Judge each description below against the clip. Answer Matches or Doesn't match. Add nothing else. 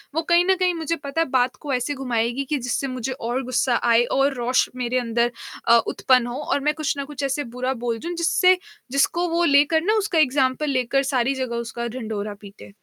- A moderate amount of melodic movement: Matches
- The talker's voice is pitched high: Matches